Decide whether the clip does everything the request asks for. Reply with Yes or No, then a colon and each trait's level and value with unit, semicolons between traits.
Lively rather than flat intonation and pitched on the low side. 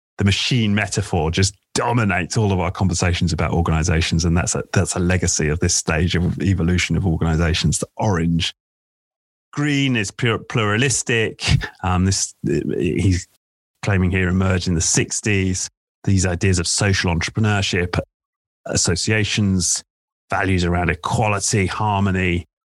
No: average, 2.9 semitones; very low, 95 Hz